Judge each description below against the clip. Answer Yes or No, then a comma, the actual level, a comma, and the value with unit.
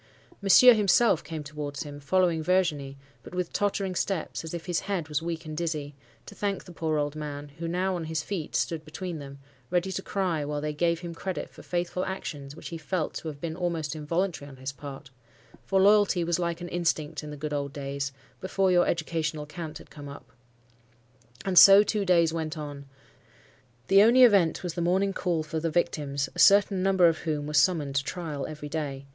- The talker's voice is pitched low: No, medium, 165 Hz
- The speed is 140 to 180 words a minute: No, fast, 205 wpm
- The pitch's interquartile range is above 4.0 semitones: No, average, 3.5 semitones